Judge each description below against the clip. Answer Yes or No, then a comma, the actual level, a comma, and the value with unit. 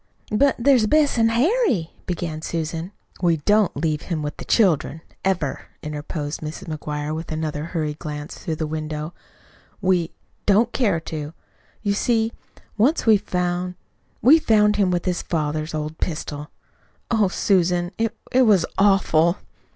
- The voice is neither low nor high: Yes, medium, 175 Hz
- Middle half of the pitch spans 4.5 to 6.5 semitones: Yes, average, 5.2 semitones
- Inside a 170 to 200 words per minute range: No, average, 145 wpm